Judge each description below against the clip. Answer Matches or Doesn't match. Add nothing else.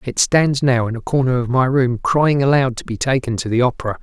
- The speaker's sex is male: Matches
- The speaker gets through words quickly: Matches